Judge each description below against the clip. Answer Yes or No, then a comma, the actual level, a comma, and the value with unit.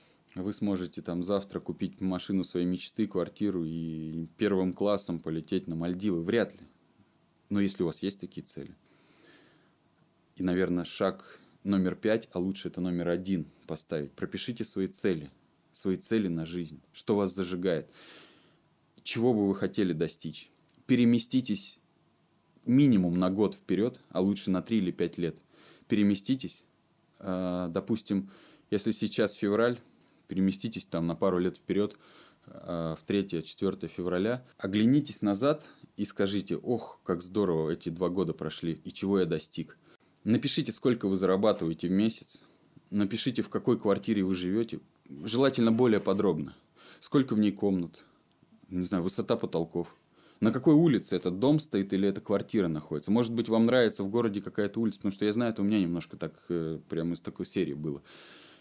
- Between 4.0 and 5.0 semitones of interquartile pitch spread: No, average, 3.6 semitones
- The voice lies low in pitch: Yes, very low, 95 Hz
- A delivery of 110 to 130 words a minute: No, average, 150 wpm